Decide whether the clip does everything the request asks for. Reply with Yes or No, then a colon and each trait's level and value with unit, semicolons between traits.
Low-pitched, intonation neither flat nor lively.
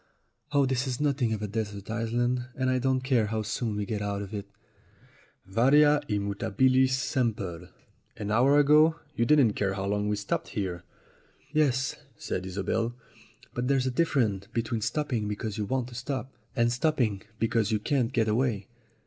Yes: low, 115 Hz; average, 4.1 semitones